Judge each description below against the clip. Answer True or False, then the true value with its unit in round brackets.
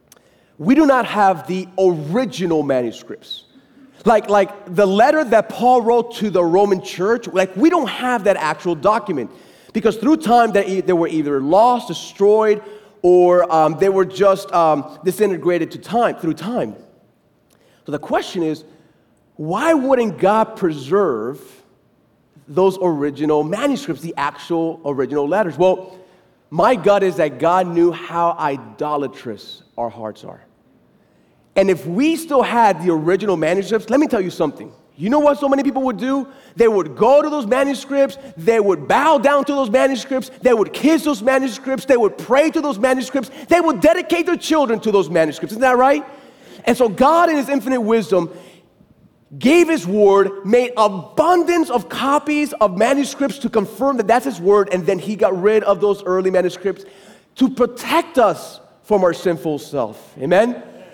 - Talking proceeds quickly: False (165 wpm)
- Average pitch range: False (6.8 semitones)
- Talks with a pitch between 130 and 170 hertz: False (210 Hz)